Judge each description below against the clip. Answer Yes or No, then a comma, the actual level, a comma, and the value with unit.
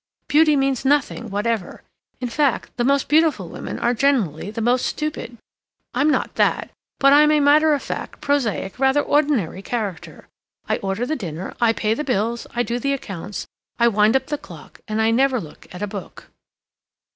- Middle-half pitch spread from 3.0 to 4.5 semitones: No, average, 5.1 semitones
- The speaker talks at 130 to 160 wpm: No, average, 180 wpm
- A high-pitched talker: Yes, high, 240 Hz